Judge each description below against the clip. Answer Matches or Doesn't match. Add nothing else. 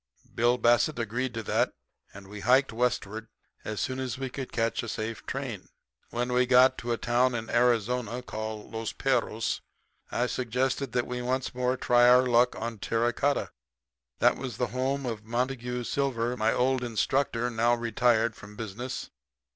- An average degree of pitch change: Doesn't match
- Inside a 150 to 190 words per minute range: Matches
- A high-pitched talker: Doesn't match